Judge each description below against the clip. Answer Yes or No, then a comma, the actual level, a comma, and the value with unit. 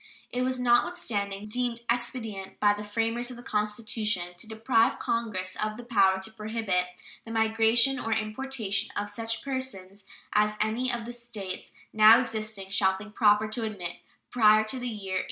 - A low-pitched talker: No, high, 220 Hz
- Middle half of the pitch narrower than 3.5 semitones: Yes, narrow, 2.5 semitones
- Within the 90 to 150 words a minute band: No, average, 170 wpm